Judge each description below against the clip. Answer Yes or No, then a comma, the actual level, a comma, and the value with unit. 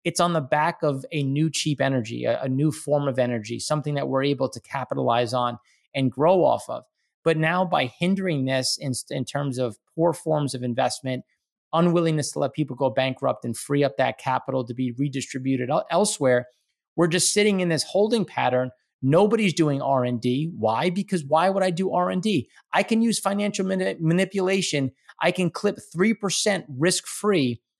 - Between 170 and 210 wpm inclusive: Yes, average, 175 wpm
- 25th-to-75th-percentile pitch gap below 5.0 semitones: No, wide, 5.5 semitones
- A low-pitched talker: No, medium, 150 Hz